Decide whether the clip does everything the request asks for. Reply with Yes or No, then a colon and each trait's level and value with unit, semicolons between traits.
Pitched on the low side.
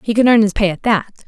No: high, 215 Hz